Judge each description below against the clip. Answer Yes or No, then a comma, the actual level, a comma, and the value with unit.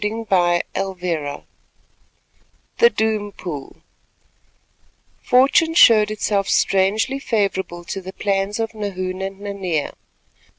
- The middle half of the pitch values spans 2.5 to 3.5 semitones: Yes, average, 2.8 semitones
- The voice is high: Yes, high, 195 Hz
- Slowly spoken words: Yes, slow, 95 wpm